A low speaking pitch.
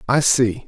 Yes: low, 125 Hz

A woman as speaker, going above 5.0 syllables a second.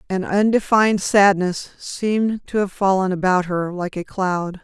No: female; 4.4 syllables/s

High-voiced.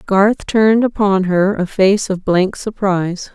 Yes: high, 195 Hz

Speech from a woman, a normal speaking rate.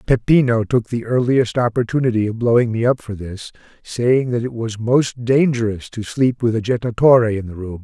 No: male; average, 190 wpm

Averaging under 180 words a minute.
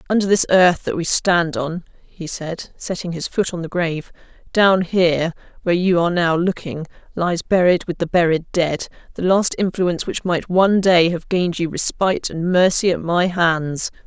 No: average, 190 wpm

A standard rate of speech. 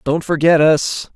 Yes: average, 155 wpm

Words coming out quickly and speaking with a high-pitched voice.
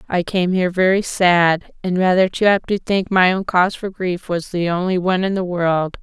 No: fast, 230 wpm; medium, 180 Hz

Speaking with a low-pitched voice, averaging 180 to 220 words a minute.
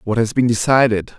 Yes: low, 115 Hz; average, 200 wpm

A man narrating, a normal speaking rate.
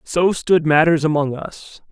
Yes: male; average, 155 wpm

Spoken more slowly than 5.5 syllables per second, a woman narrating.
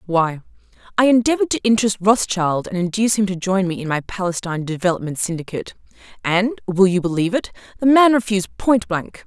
No: 6.2 syllables/s; female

